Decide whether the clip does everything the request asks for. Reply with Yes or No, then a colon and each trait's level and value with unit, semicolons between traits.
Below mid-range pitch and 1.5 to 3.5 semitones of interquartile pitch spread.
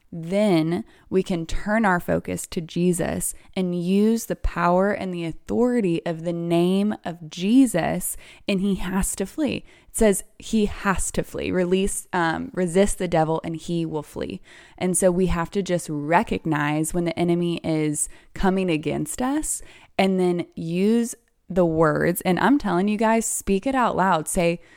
No: medium, 180 Hz; average, 3.0 semitones